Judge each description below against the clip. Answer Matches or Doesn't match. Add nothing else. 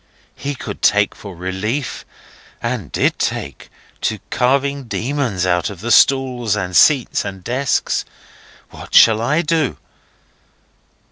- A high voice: Doesn't match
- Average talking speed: Doesn't match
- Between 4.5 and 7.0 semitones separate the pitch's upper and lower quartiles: Matches